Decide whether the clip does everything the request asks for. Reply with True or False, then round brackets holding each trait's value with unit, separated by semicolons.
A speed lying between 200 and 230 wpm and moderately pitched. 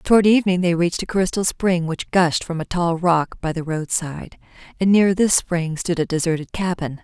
True (205 wpm; 175 Hz)